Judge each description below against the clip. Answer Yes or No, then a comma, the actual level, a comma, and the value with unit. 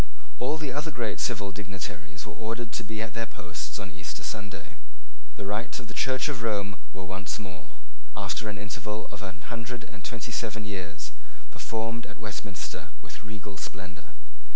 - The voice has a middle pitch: No, low, 105 Hz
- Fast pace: No, average, 175 wpm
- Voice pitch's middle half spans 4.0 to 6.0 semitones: No, average, 2.9 semitones